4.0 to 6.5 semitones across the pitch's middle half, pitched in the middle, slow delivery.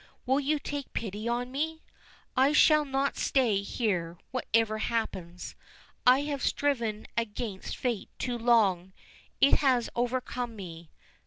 No: average, 4.3 semitones; high, 240 Hz; slow, 130 wpm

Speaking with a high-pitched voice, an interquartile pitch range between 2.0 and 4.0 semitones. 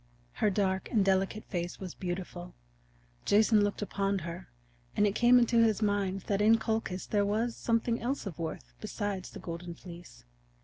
Yes: high, 200 Hz; average, 3.1 semitones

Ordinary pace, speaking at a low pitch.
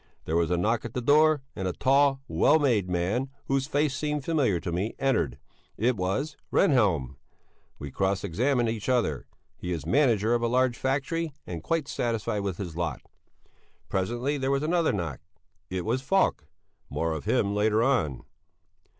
Yes: average, 170 wpm; low, 115 Hz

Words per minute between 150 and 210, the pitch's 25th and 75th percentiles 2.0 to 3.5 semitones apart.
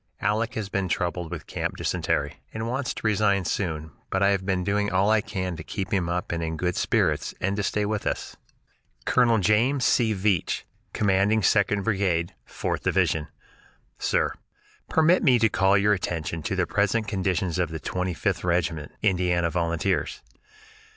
Yes: average, 170 wpm; average, 3.2 semitones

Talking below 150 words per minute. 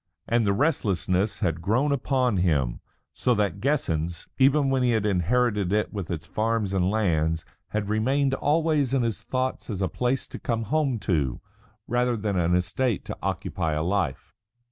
No: average, 170 wpm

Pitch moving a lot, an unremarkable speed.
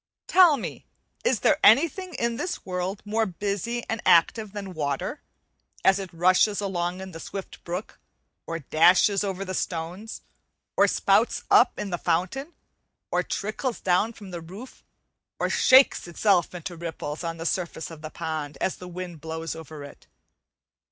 No: average, 4.1 semitones; average, 160 wpm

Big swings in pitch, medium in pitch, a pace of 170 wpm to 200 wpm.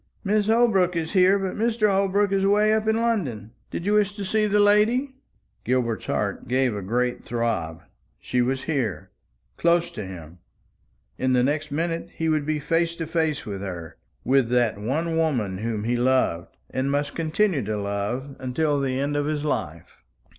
Yes: wide, 8.2 semitones; medium, 145 Hz; average, 180 wpm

